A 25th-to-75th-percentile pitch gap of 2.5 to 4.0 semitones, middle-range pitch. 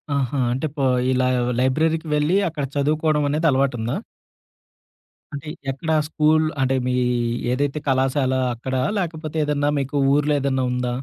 Yes: average, 2.8 semitones; medium, 145 Hz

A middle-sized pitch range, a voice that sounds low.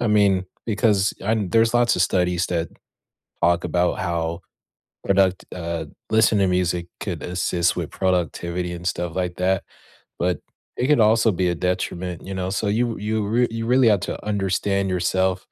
Yes: average, 3.2 semitones; very low, 95 Hz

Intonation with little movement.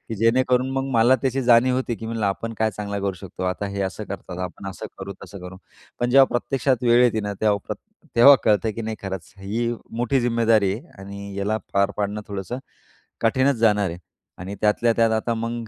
No: average, 3.2 semitones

